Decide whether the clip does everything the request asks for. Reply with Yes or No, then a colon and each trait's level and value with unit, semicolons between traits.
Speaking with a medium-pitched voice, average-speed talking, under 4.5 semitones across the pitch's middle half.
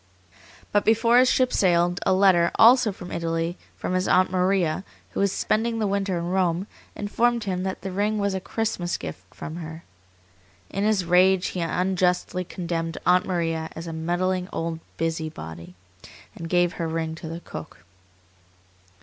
Yes: medium, 180 Hz; average, 165 wpm; average, 2.9 semitones